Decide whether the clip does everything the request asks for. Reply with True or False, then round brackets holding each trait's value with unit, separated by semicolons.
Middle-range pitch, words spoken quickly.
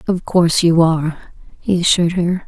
False (170 Hz; 170 wpm)